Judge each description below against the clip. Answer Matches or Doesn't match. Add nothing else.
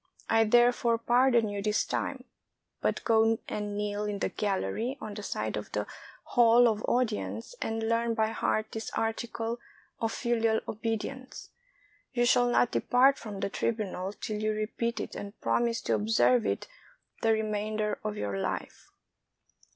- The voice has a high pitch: Matches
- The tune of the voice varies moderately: Doesn't match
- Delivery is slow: Doesn't match